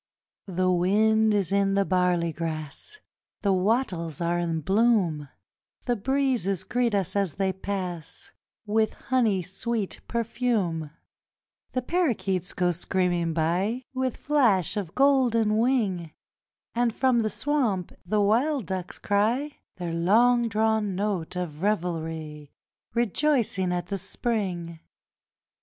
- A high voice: Yes, high, 200 Hz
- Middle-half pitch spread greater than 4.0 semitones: Yes, average, 4.9 semitones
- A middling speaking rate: No, slow, 120 wpm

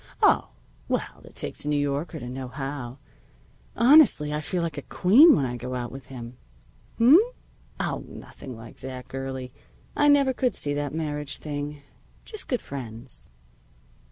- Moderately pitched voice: Yes, medium, 145 Hz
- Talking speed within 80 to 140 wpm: No, average, 160 wpm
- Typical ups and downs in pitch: Yes, average, 4.5 semitones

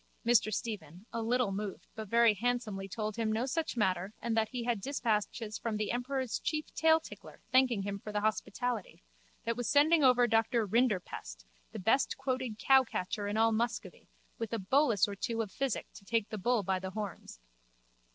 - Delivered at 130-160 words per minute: No, average, 180 wpm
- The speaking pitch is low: No, high, 225 Hz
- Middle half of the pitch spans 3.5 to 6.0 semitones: No, average, 3.1 semitones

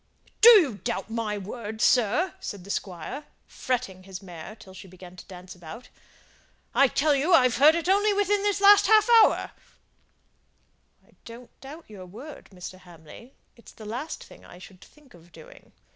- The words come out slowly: No, average, 180 wpm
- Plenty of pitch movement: Yes, wide, 8.5 semitones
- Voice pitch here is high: Yes, high, 230 Hz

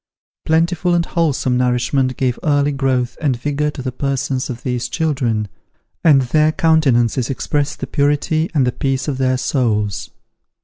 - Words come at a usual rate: Yes, average, 150 wpm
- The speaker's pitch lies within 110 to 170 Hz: Yes, low, 135 Hz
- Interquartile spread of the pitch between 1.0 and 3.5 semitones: Yes, average, 3.1 semitones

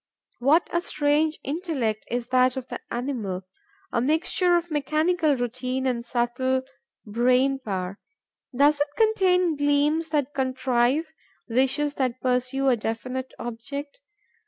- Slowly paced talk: Yes, slow, 125 wpm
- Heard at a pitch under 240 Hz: No, very high, 265 Hz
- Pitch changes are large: No, average, 3.5 semitones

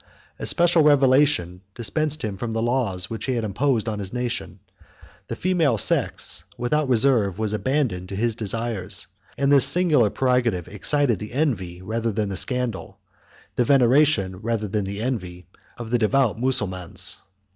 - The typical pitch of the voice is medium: No, low, 115 Hz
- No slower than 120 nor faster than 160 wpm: Yes, average, 155 wpm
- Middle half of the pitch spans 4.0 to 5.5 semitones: Yes, average, 4.9 semitones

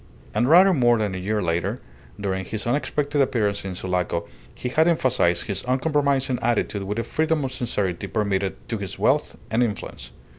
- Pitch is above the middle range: No, low, 110 Hz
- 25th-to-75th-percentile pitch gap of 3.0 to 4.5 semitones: No, wide, 5.6 semitones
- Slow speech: No, average, 175 wpm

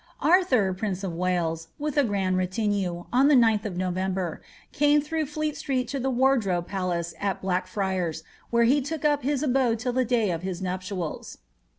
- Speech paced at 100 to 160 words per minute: No, average, 185 wpm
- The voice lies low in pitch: No, high, 205 Hz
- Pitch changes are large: Yes, wide, 6.5 semitones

